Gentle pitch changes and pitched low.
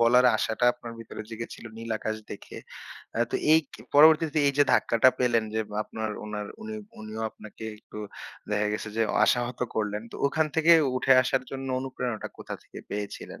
No: average, 3.4 semitones; low, 115 Hz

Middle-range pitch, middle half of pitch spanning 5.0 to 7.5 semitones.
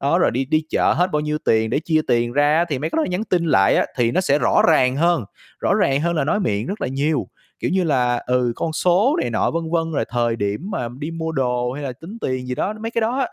Yes: medium, 150 Hz; average, 5.3 semitones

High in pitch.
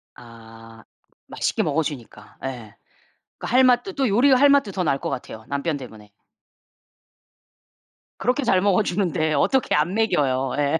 No: medium, 155 Hz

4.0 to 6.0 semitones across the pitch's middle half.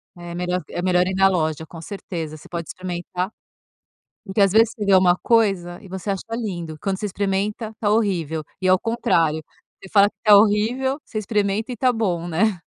No: average, 3.2 semitones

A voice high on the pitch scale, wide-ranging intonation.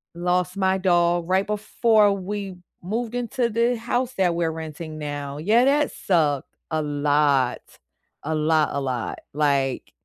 No: medium, 175 Hz; wide, 5.8 semitones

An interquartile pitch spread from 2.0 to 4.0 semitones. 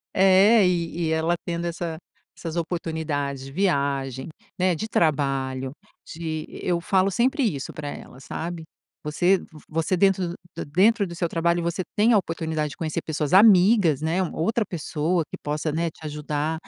Yes: average, 3.4 semitones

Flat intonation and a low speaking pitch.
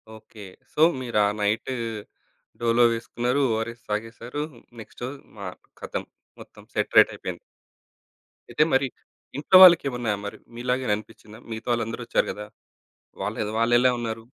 Yes: narrow, 2.3 semitones; low, 115 Hz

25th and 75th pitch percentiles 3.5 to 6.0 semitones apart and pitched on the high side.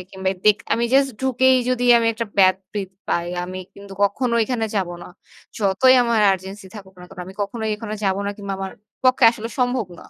Yes: average, 4.0 semitones; high, 210 Hz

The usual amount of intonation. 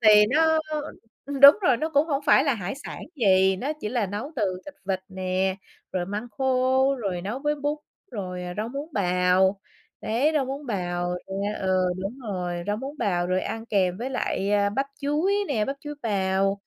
No: wide, 6.4 semitones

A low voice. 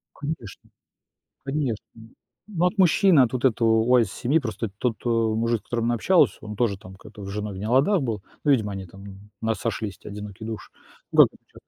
Yes: low, 115 Hz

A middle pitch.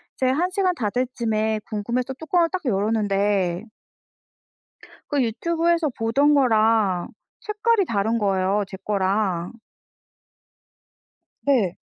No: high, 225 Hz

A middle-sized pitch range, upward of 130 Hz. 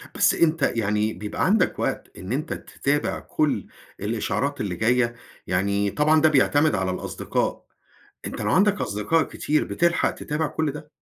No: wide, 6.9 semitones; medium, 140 Hz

